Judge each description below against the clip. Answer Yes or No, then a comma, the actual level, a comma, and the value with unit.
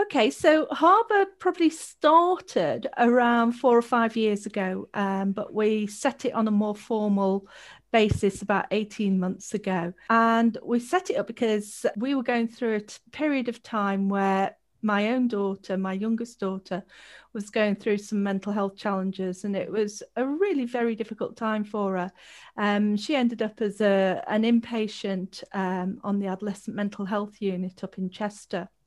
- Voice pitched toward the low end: No, high, 215 Hz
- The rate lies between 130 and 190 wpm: Yes, average, 170 wpm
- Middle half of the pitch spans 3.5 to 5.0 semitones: No, average, 3.1 semitones